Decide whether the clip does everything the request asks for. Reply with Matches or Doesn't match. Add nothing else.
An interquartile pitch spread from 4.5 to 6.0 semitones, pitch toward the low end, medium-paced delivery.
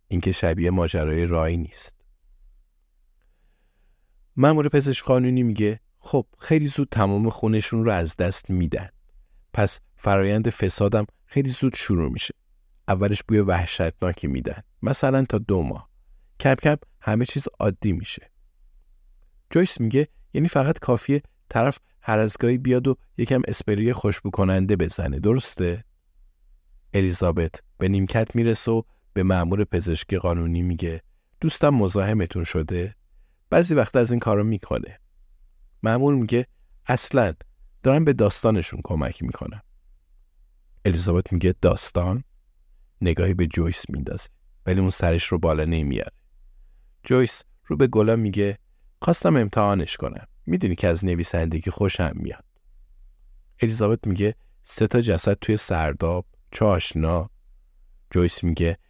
Matches